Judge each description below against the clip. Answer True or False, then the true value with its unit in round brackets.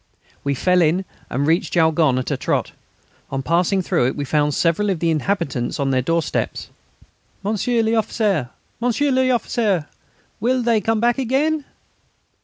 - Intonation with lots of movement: True (7.0 semitones)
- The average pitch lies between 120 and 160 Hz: False (185 Hz)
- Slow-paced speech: False (150 wpm)